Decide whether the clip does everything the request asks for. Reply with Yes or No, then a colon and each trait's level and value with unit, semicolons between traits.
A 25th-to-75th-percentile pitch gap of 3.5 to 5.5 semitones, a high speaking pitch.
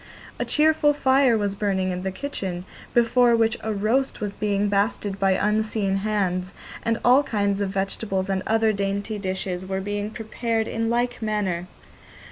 No: average, 2.7 semitones; high, 205 Hz